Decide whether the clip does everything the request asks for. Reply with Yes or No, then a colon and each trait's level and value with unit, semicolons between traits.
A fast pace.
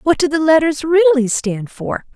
No: average, 195 wpm